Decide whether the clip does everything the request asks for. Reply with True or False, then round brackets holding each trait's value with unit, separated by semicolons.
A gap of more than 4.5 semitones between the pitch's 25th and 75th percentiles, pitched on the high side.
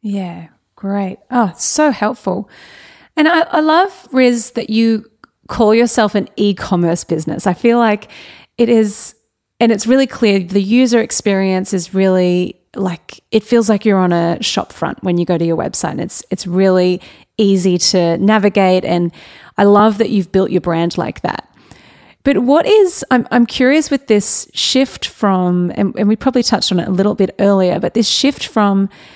False (4.2 semitones; 205 Hz)